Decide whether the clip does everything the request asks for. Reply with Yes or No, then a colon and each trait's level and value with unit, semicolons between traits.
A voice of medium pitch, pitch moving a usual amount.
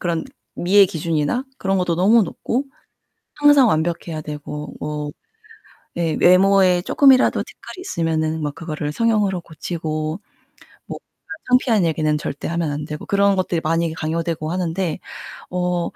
Yes: medium, 170 Hz; average, 3.7 semitones